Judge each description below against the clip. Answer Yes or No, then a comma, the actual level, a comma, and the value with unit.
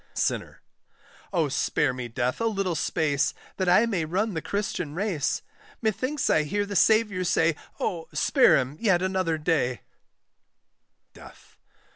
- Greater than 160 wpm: No, average, 140 wpm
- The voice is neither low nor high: Yes, medium, 175 Hz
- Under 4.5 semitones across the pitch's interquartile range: No, average, 5.2 semitones